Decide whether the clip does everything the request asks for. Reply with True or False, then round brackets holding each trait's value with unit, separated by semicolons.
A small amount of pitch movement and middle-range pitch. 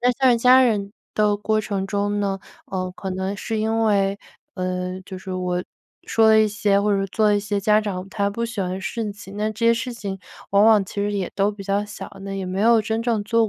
False (2.0 semitones; 205 Hz)